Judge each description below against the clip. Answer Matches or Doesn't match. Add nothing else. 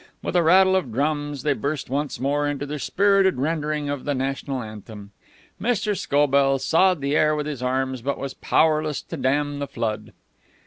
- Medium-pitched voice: Matches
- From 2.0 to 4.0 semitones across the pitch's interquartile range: Matches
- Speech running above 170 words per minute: Matches